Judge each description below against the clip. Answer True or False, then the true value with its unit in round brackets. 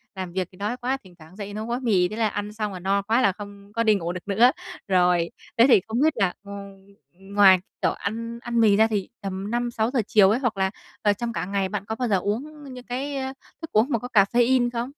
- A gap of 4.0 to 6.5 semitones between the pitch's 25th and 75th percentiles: False (3.5 semitones)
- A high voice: True (210 Hz)